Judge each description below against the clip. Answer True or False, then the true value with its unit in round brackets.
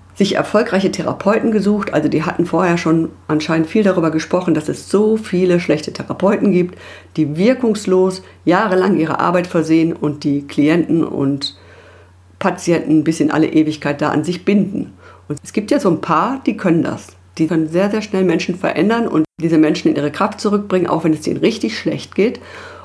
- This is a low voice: False (170 Hz)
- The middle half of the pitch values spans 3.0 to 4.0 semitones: True (3.6 semitones)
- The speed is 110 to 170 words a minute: False (185 wpm)